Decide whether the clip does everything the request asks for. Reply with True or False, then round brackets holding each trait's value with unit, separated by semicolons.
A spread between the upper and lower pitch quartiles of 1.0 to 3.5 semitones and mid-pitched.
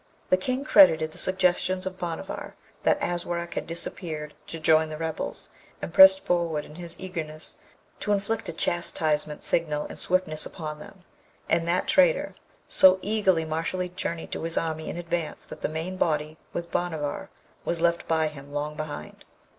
True (2.9 semitones; 170 Hz)